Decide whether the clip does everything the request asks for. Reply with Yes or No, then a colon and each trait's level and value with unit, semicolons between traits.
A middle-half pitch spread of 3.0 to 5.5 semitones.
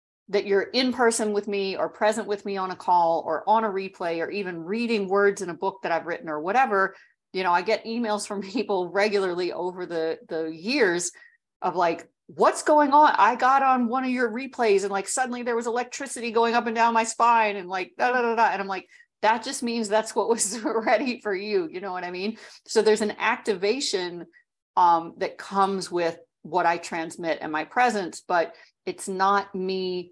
Yes: average, 4.3 semitones